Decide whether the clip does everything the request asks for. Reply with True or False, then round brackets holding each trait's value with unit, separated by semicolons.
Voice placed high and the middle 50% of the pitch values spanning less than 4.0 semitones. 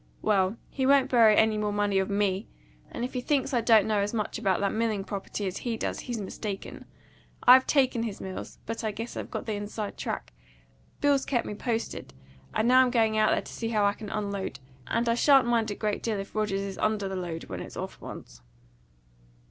True (215 Hz; 2.8 semitones)